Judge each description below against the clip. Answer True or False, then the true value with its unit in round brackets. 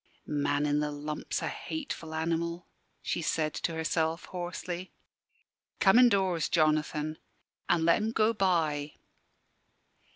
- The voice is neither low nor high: True (165 Hz)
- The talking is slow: True (120 wpm)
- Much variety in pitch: False (2.9 semitones)